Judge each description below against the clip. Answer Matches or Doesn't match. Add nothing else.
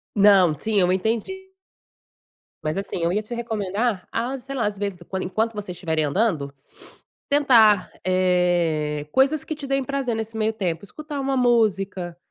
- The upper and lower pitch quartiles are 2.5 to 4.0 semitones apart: Doesn't match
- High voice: Matches